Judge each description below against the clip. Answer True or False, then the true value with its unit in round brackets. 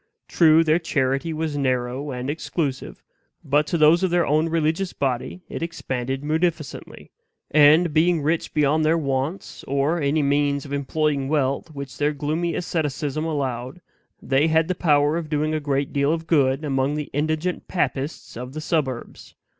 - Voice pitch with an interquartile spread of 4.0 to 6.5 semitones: False (2.7 semitones)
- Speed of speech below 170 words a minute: True (160 wpm)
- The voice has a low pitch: False (150 Hz)